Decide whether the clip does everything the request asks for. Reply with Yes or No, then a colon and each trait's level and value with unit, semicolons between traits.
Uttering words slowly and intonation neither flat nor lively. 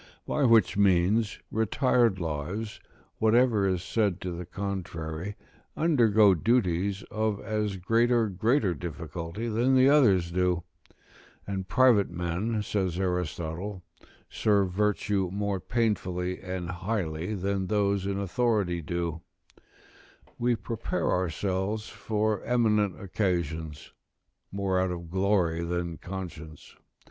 Yes: slow, 115 wpm; average, 3.6 semitones